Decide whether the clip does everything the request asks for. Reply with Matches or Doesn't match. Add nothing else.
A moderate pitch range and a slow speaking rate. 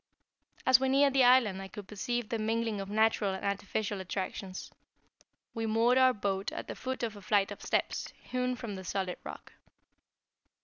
Doesn't match